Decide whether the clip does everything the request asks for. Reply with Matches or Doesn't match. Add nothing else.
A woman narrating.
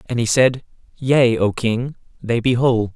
Doesn't match